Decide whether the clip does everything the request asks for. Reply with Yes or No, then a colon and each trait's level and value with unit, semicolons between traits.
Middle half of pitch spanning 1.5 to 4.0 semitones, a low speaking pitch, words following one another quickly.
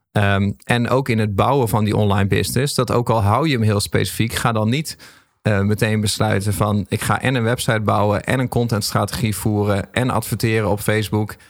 Yes: narrow, 2.5 semitones; low, 110 Hz; fast, 205 wpm